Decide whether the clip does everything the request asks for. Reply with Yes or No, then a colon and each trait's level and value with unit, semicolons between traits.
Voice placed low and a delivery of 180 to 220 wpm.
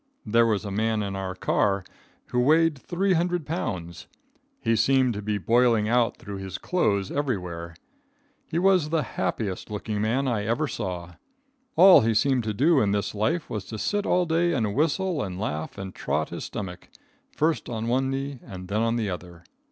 Yes: low, 115 Hz; average, 185 wpm